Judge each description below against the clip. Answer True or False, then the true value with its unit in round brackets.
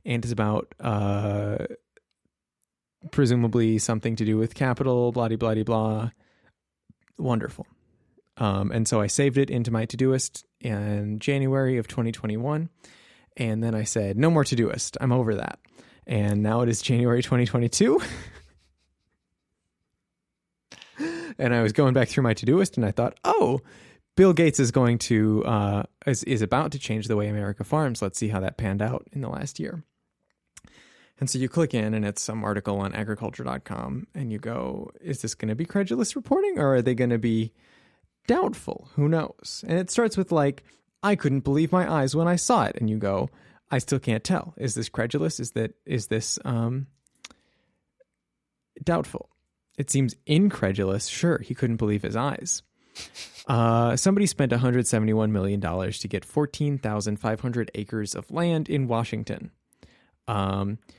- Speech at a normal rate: True (170 wpm)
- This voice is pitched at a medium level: False (115 Hz)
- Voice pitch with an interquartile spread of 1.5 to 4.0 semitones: False (4.4 semitones)